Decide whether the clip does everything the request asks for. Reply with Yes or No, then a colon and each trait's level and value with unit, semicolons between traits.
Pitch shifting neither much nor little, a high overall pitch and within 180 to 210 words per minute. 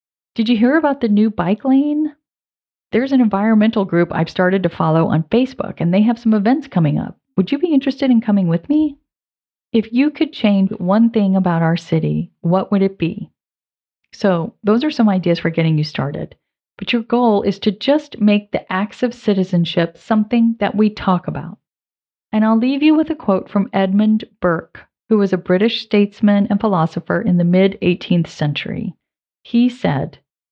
Yes: average, 4.8 semitones; high, 205 Hz; average, 185 wpm